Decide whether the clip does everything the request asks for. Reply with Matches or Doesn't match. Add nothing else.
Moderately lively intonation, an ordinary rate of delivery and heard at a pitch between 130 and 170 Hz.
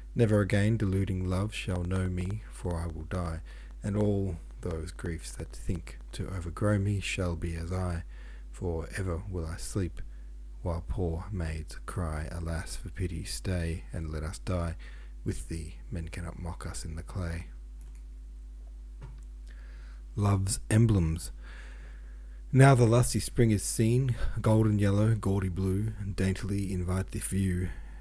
Doesn't match